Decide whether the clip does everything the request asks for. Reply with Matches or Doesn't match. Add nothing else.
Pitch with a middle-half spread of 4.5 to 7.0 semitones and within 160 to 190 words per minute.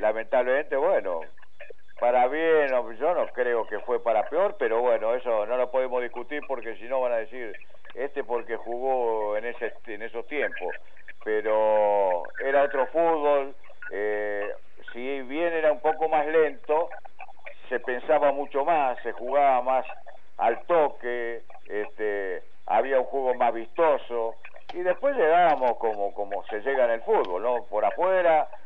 Doesn't match